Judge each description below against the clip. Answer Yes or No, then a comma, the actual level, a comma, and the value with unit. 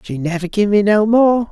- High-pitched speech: Yes, high, 205 Hz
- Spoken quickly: Yes, fast, 240 wpm